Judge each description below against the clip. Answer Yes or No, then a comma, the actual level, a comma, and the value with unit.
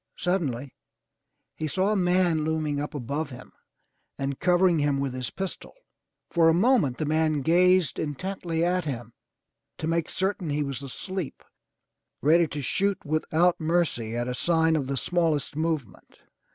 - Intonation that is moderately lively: Yes, average, 3.9 semitones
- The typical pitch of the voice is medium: Yes, medium, 160 Hz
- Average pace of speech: Yes, average, 150 wpm